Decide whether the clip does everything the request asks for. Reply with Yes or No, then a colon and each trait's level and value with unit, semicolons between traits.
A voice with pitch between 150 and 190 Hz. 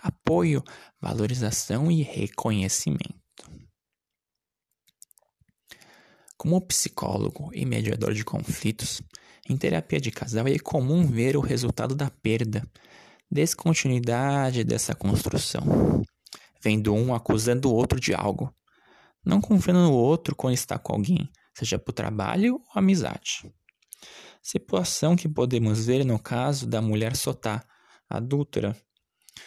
No: low, 125 Hz